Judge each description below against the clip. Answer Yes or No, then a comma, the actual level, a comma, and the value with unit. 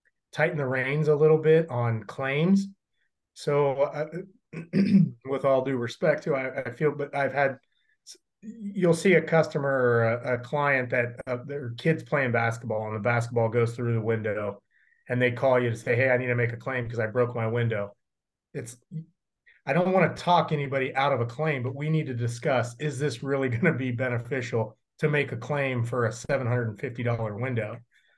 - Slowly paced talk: No, average, 195 wpm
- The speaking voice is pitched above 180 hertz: No, low, 135 Hz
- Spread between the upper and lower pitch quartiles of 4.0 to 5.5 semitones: Yes, average, 4.3 semitones